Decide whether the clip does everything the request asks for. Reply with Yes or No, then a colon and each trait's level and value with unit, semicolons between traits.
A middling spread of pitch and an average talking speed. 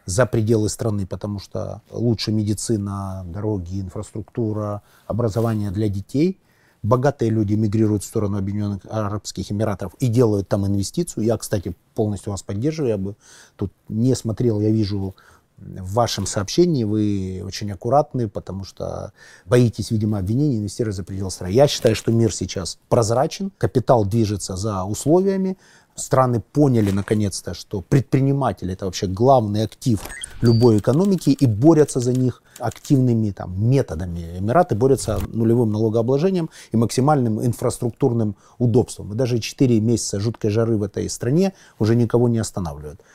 Yes: average, 3.5 semitones; average, 140 wpm